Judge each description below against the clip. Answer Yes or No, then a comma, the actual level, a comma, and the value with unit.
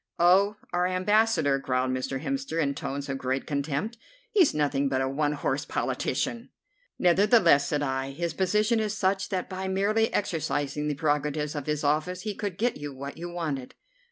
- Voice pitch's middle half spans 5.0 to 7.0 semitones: Yes, wide, 5.6 semitones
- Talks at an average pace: Yes, average, 175 wpm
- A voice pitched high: No, medium, 155 Hz